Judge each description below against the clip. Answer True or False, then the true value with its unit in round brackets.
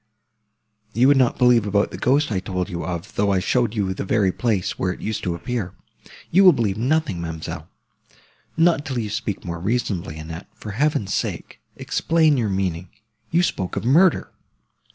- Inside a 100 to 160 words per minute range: False (175 wpm)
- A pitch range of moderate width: False (5.7 semitones)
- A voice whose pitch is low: True (105 Hz)